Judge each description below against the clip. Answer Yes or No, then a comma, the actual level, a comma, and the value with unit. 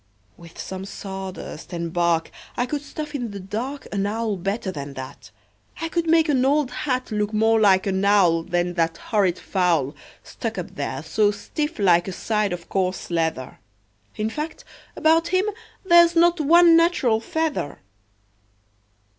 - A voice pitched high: Yes, high, 210 Hz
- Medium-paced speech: Yes, average, 160 wpm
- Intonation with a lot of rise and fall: Yes, wide, 8.7 semitones